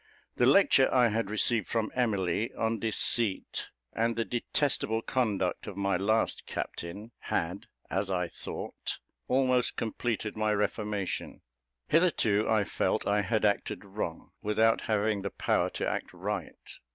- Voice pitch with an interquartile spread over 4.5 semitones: No, narrow, 2.6 semitones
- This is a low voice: Yes, low, 110 Hz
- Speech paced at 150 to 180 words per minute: No, average, 140 wpm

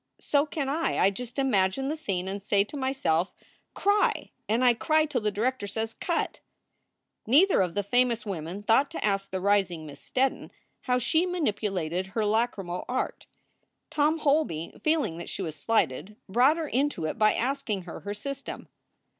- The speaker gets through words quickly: No, average, 175 wpm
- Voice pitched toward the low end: No, high, 225 Hz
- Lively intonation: Yes, wide, 6.3 semitones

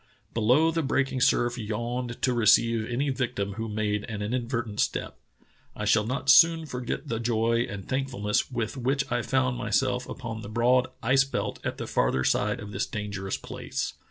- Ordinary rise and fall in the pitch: Yes, average, 3.2 semitones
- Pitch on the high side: No, low, 120 Hz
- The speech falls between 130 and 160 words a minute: No, average, 175 wpm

